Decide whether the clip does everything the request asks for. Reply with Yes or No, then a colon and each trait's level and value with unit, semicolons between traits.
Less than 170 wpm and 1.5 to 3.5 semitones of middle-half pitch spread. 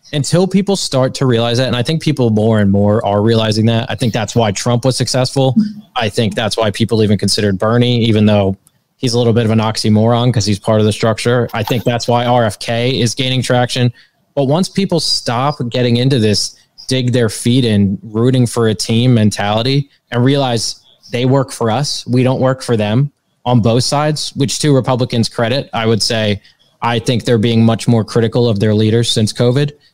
No: fast, 205 wpm; average, 2.8 semitones